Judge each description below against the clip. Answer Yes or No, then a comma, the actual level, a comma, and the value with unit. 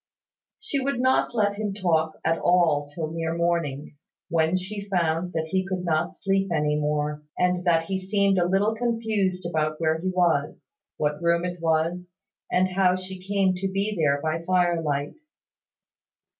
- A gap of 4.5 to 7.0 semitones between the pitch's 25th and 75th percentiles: No, average, 3.3 semitones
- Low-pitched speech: No, medium, 175 Hz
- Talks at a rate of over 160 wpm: Yes, average, 170 wpm